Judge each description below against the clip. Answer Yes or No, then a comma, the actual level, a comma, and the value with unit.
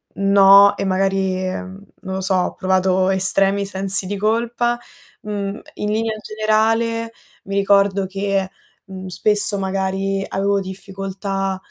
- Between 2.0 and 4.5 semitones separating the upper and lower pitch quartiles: No, narrow, 1.2 semitones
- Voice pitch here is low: No, high, 195 Hz